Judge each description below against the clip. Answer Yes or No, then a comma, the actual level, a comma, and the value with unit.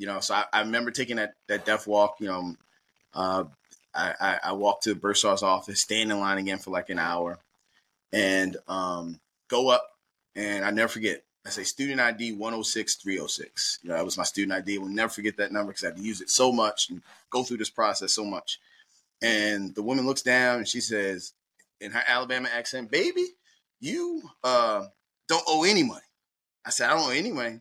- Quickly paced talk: Yes, fast, 215 wpm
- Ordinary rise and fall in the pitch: Yes, average, 4.0 semitones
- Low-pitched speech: Yes, low, 105 Hz